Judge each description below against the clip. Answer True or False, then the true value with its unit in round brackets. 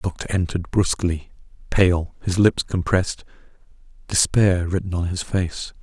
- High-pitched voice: False (90 Hz)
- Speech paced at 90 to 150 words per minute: True (135 wpm)